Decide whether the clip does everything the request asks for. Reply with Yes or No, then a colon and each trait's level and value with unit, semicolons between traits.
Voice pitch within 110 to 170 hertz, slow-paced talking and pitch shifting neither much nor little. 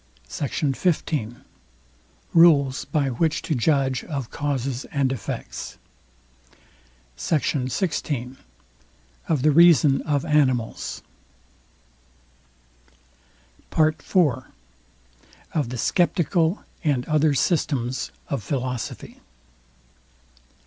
Yes: medium, 140 Hz; slow, 80 wpm; average, 3.5 semitones